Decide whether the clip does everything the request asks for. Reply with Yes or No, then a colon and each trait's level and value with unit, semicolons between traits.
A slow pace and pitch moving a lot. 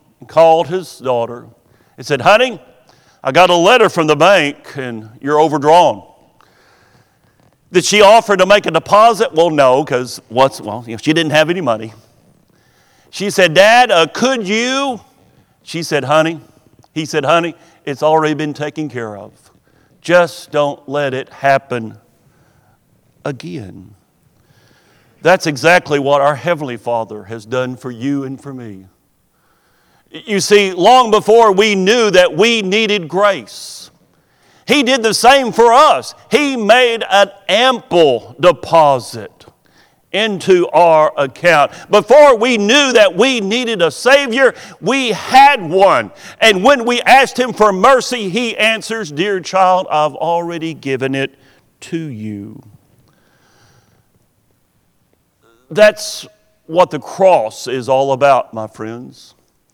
Yes: slow, 130 wpm; wide, 7.8 semitones